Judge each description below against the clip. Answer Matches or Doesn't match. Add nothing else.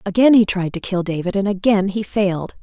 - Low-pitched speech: Doesn't match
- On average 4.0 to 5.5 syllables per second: Doesn't match